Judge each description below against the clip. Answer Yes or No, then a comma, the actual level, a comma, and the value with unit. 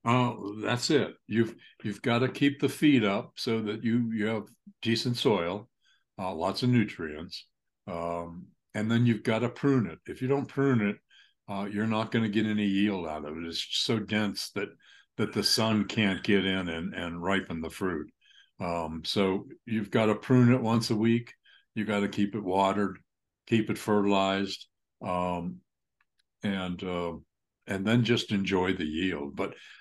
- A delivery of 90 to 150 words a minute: No, average, 185 wpm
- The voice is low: Yes, low, 105 Hz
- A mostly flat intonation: No, average, 3.6 semitones